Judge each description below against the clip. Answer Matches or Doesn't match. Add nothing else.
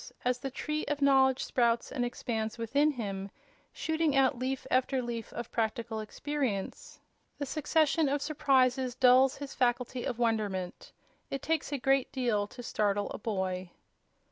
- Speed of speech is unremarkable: Matches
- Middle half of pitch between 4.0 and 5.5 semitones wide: Doesn't match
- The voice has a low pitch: Doesn't match